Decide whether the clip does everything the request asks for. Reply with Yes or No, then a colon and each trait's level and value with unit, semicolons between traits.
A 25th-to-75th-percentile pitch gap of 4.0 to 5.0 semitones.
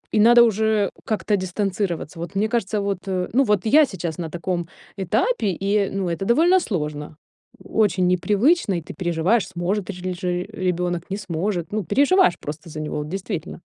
No: average, 3.6 semitones